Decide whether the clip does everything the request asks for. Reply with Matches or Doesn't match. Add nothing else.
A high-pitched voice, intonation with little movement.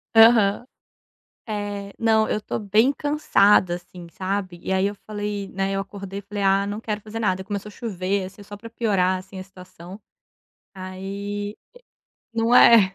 Matches